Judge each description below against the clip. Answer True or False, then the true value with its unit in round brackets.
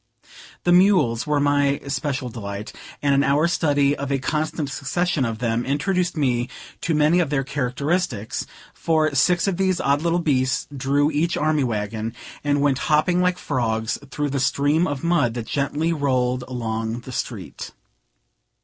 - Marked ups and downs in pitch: False (3.7 semitones)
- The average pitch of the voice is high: False (140 Hz)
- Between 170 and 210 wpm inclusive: False (160 wpm)